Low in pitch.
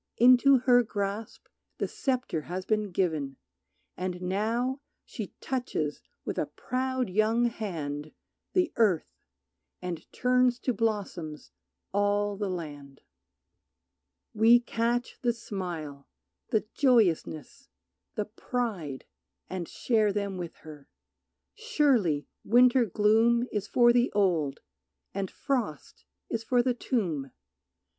No: high, 210 Hz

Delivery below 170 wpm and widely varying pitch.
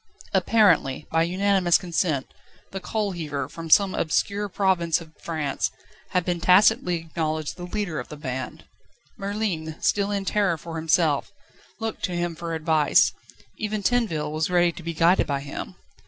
No: average, 155 wpm; average, 3.7 semitones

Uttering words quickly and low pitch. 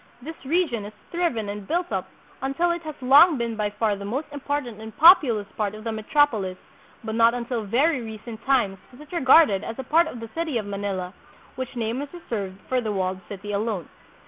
No: fast, 210 wpm; high, 235 Hz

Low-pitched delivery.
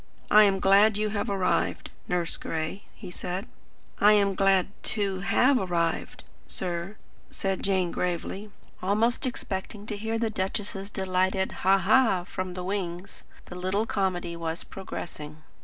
No: high, 195 Hz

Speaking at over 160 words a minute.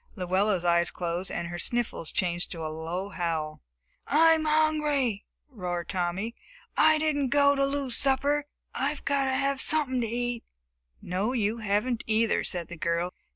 No: average, 155 wpm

